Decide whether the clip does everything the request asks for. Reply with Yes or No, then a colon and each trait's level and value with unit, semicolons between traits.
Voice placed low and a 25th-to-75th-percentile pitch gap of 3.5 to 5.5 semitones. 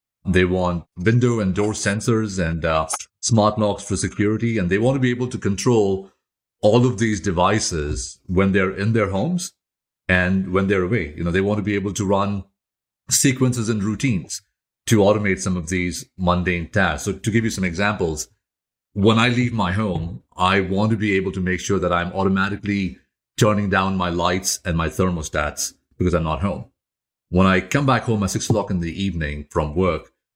No: very low, 95 Hz; average, 2.9 semitones